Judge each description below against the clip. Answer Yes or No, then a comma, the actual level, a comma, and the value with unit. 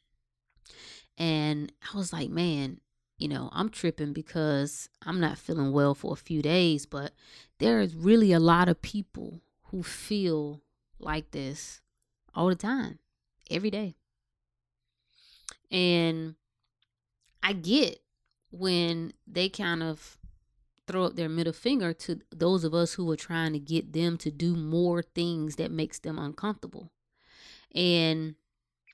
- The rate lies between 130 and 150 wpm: Yes, slow, 135 wpm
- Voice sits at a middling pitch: Yes, medium, 165 Hz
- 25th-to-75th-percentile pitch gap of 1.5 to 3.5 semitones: Yes, average, 3.2 semitones